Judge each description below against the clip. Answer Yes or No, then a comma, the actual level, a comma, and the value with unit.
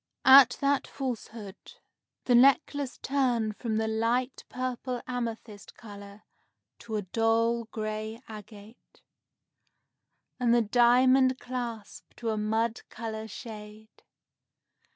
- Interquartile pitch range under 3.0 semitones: Yes, narrow, 2.5 semitones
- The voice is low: No, high, 230 Hz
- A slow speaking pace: Yes, slow, 105 wpm